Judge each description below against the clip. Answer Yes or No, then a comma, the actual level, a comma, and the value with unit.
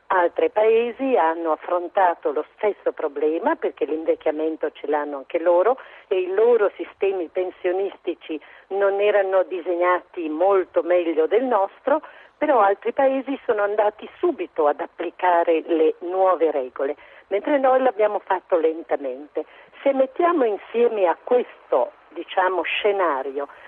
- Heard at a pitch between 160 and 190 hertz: Yes, medium, 185 Hz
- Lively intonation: Yes, wide, 7.7 semitones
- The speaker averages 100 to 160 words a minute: Yes, average, 120 wpm